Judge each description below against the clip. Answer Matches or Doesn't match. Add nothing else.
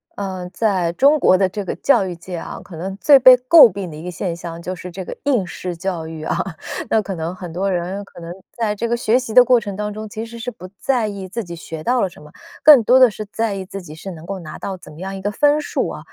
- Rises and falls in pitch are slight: Doesn't match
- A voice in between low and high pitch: Doesn't match